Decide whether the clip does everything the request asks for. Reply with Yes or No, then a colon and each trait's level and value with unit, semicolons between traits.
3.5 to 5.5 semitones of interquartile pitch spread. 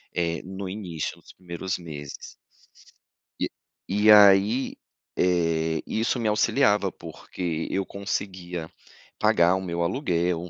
No: average, 2.9 semitones